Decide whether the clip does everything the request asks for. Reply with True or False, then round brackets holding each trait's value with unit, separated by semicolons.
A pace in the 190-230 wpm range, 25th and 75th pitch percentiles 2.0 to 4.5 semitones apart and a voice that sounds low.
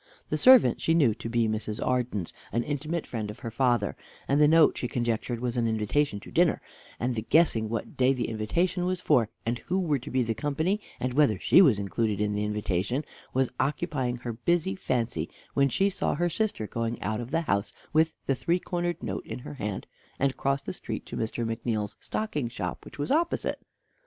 False (205 wpm; 5.4 semitones; 125 Hz)